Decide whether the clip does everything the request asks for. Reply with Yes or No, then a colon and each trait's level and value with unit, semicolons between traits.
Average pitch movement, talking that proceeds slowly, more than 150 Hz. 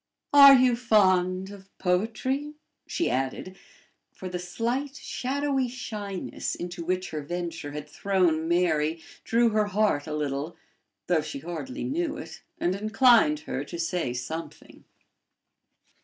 No: wide, 6.3 semitones; slow, 130 wpm; medium, 185 Hz